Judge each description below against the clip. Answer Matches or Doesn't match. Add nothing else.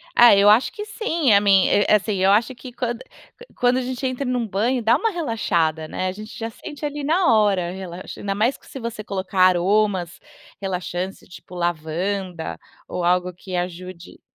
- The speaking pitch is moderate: Doesn't match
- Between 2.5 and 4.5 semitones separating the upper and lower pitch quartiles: Doesn't match